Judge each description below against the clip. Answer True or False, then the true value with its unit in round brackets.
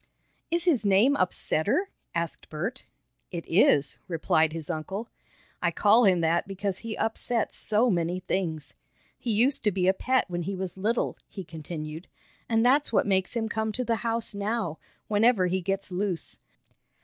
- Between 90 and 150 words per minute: False (165 wpm)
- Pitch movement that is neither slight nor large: True (4.8 semitones)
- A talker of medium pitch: False (195 Hz)